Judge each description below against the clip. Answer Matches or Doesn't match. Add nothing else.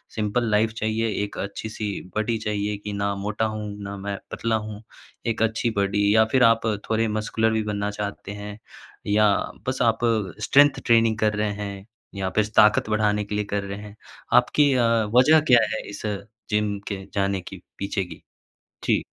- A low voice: Matches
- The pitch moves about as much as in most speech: Doesn't match